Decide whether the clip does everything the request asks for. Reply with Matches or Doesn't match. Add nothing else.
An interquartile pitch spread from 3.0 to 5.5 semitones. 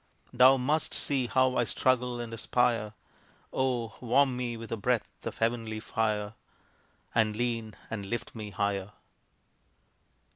Doesn't match